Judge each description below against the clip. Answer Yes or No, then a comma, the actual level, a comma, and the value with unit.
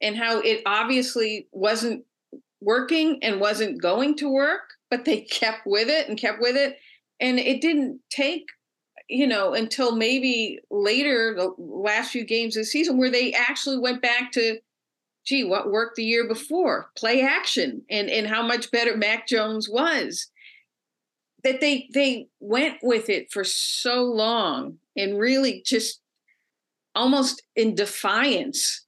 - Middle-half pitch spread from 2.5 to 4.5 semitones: Yes, average, 3.7 semitones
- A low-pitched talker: No, high, 245 Hz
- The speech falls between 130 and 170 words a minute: Yes, average, 150 wpm